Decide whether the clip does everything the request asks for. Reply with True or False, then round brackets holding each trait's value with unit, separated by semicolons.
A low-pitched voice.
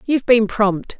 False (225 Hz)